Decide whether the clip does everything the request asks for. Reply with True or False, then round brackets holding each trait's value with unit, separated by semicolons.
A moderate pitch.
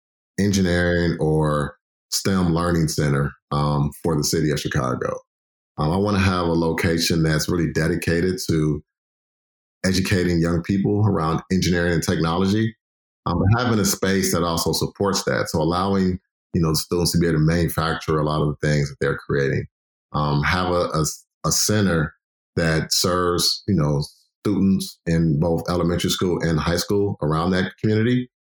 False (85 Hz)